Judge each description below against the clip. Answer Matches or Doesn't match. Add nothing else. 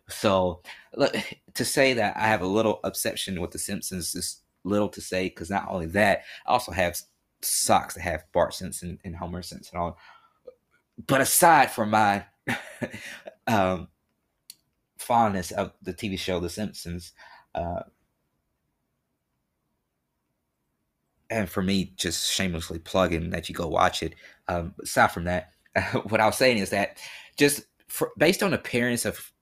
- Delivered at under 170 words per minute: Matches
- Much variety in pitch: Doesn't match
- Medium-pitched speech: Doesn't match